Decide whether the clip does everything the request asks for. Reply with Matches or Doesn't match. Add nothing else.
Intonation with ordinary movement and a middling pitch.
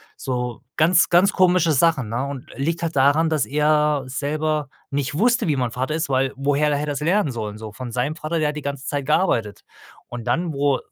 Matches